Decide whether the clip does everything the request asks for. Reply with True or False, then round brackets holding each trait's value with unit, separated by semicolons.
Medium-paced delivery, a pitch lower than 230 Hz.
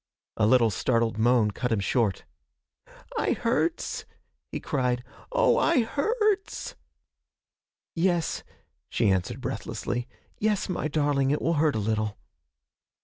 False (120 wpm; 135 Hz)